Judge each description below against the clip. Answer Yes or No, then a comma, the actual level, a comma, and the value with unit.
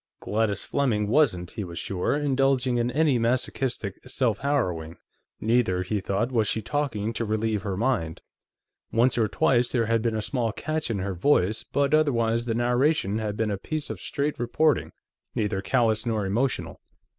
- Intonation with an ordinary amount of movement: Yes, average, 4.0 semitones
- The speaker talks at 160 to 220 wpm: Yes, average, 170 wpm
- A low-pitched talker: Yes, low, 115 Hz